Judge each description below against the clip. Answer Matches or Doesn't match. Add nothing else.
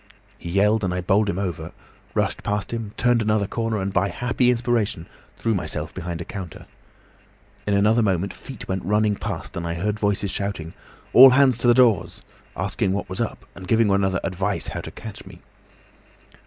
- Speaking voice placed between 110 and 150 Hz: Doesn't match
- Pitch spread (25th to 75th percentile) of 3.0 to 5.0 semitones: Matches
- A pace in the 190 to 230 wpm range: Matches